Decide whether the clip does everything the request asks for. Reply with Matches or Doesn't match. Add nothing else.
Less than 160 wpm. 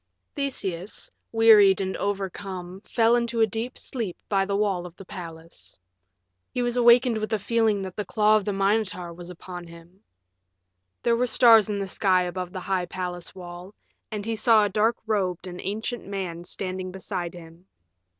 Doesn't match